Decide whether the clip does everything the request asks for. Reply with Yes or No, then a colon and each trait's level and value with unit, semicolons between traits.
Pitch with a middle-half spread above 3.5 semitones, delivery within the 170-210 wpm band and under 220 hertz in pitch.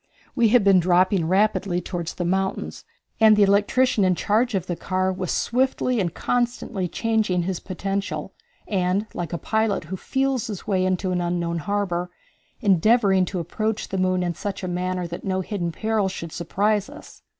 No: average, 3.1 semitones; average, 175 wpm; high, 190 Hz